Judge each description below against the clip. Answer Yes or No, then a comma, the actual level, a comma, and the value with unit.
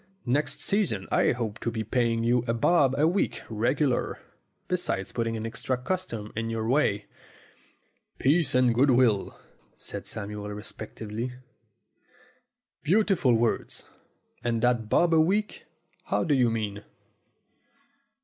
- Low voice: Yes, low, 120 Hz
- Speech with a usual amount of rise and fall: Yes, average, 4.3 semitones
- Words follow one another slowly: Yes, slow, 125 wpm